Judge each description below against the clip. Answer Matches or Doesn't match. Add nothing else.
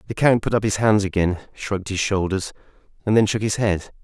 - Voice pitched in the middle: Doesn't match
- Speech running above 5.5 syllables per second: Matches